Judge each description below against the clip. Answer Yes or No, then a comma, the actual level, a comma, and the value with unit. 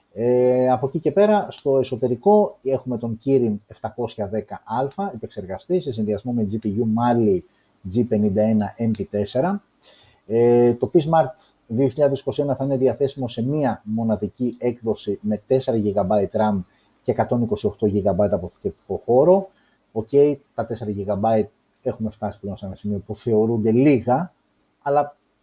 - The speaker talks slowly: No, average, 125 wpm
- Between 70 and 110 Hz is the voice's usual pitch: No, low, 120 Hz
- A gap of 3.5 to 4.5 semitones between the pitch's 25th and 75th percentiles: Yes, average, 4.2 semitones